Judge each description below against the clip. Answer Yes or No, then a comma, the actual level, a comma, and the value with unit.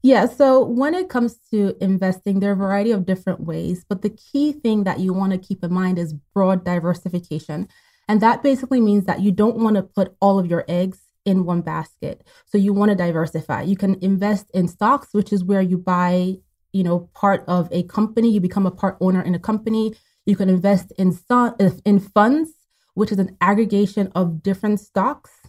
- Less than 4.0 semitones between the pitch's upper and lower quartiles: Yes, narrow, 2.5 semitones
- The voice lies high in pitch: Yes, high, 195 Hz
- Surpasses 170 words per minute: Yes, fast, 205 wpm